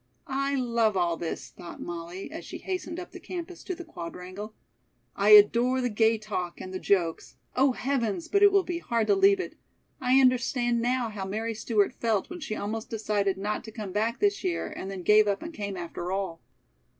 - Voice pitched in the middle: No, high, 225 Hz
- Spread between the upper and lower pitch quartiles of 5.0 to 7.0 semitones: Yes, wide, 5.5 semitones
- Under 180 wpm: No, fast, 205 wpm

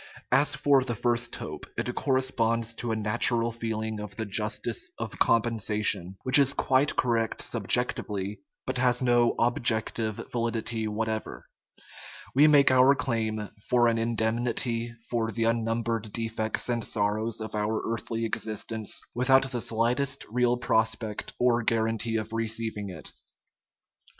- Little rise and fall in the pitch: Yes, narrow, 1.7 semitones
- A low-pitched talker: Yes, low, 115 Hz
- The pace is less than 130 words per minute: No, slow, 135 wpm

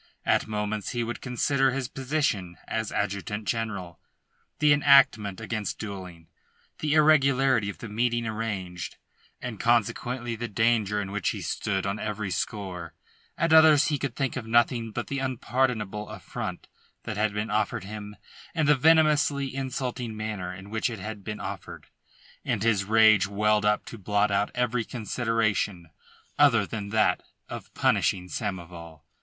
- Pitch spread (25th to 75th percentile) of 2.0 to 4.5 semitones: Yes, average, 3.6 semitones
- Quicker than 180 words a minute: No, average, 150 wpm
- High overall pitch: No, low, 110 Hz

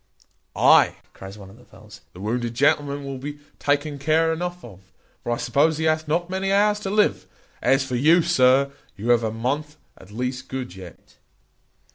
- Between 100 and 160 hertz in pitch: Yes, medium, 140 Hz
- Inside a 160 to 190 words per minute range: Yes, average, 185 wpm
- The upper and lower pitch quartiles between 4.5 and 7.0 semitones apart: Yes, average, 5.0 semitones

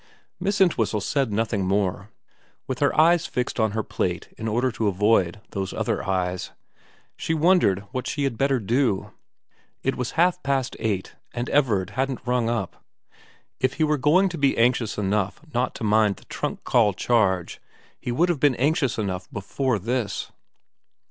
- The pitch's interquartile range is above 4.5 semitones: Yes, average, 5.0 semitones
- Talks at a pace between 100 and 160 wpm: No, average, 170 wpm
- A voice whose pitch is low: Yes, low, 120 Hz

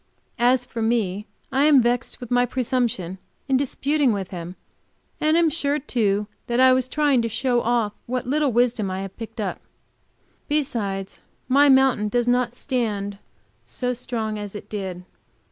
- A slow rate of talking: No, average, 160 wpm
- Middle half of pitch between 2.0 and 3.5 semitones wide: No, average, 3.9 semitones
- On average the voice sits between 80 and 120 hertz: No, high, 240 Hz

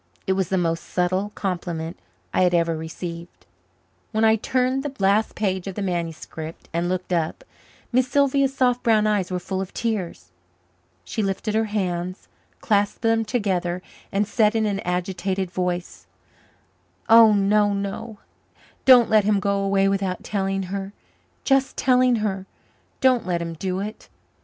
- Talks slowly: No, average, 155 wpm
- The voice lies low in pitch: No, high, 195 Hz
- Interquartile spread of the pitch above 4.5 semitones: No, average, 3.4 semitones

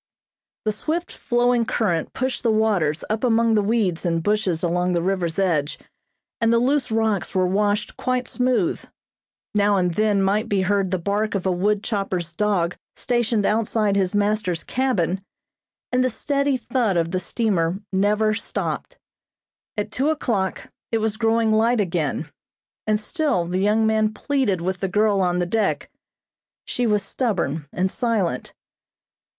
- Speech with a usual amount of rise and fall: Yes, average, 3.6 semitones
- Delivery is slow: No, average, 155 wpm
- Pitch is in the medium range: No, high, 210 Hz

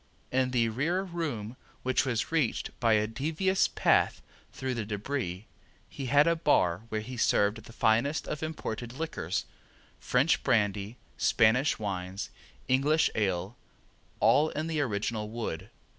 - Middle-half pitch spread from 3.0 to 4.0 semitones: No, average, 5.3 semitones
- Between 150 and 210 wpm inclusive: No, average, 140 wpm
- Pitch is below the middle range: Yes, low, 120 Hz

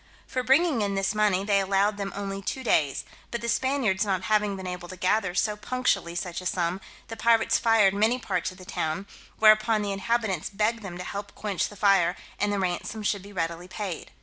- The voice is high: Yes, high, 200 Hz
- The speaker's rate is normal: No, fast, 210 wpm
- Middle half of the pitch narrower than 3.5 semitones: Yes, average, 2.7 semitones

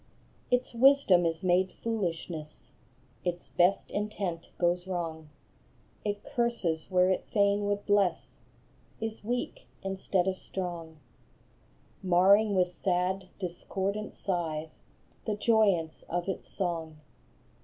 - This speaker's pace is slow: Yes, slow, 110 wpm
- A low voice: No, medium, 185 Hz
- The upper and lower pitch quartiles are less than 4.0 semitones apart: Yes, average, 2.9 semitones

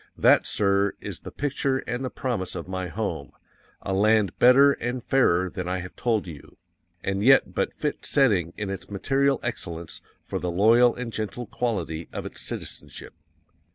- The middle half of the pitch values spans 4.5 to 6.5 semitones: Yes, average, 5.0 semitones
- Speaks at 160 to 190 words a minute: Yes, average, 170 wpm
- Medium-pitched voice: No, low, 105 Hz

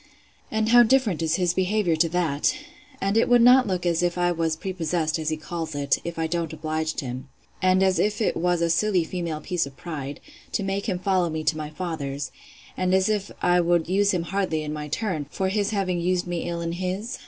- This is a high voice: No, medium, 175 Hz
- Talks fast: Yes, fast, 225 wpm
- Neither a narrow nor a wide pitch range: Yes, average, 3.2 semitones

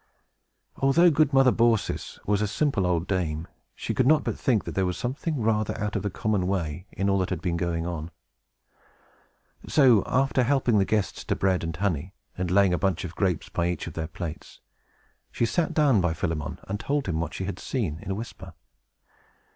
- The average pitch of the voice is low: Yes, very low, 95 Hz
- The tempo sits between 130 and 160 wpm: No, fast, 205 wpm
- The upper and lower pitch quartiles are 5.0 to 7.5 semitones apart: Yes, average, 5.3 semitones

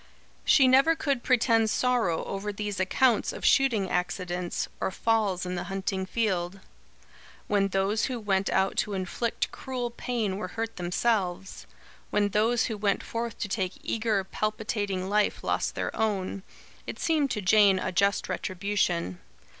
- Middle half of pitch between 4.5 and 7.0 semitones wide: No, average, 3.2 semitones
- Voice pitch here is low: No, high, 205 Hz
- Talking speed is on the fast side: No, average, 150 wpm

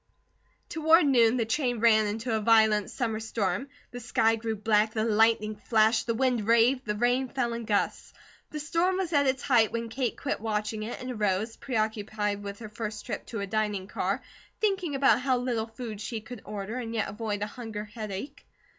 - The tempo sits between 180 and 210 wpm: Yes, average, 195 wpm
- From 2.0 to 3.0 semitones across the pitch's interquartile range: Yes, average, 2.7 semitones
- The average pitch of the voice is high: Yes, high, 225 Hz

